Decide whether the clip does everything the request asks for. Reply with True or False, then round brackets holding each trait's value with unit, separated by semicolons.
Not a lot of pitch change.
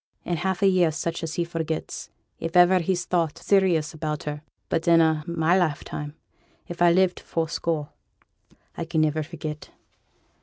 True (2.0 semitones)